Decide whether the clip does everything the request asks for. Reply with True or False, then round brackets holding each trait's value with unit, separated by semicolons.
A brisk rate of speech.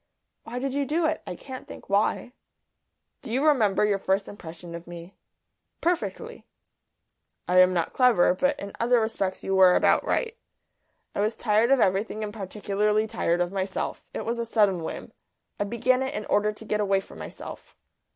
False (180 wpm)